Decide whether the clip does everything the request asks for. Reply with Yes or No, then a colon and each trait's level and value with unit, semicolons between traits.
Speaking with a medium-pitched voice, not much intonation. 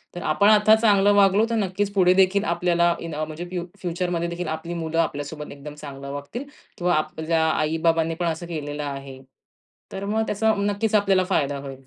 No: medium, 170 Hz; average, 4.2 semitones